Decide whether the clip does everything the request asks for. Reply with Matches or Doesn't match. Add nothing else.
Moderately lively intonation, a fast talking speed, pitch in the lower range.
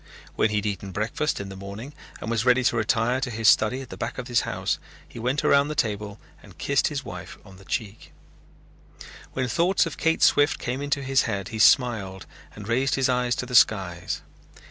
Matches